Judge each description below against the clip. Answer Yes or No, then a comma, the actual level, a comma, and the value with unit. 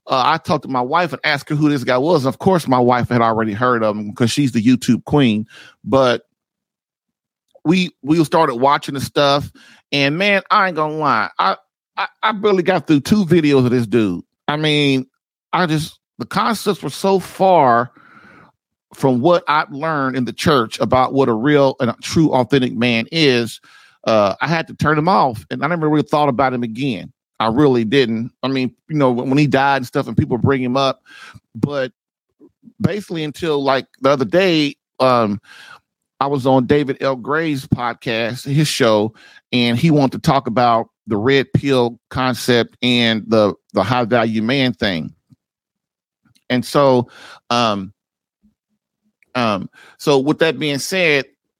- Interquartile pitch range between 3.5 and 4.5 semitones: Yes, average, 3.8 semitones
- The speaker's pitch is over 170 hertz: No, low, 135 Hz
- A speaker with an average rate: Yes, average, 175 wpm